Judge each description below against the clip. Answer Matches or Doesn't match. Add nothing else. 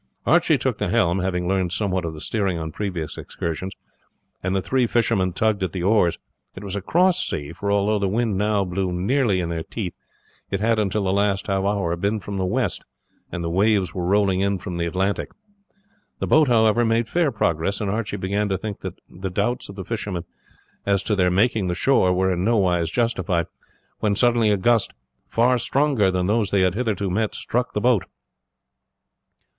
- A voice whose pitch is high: Doesn't match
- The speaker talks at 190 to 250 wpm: Matches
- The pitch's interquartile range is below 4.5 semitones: Matches